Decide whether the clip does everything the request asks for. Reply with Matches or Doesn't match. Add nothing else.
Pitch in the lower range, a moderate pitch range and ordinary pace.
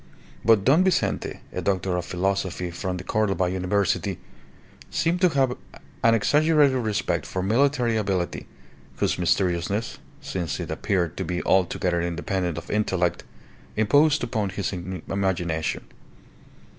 Doesn't match